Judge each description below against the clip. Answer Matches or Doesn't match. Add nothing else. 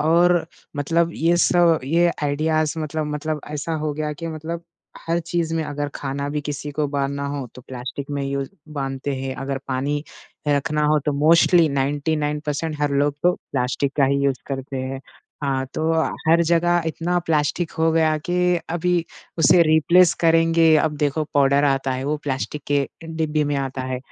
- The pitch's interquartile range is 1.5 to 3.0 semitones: Matches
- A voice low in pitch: Doesn't match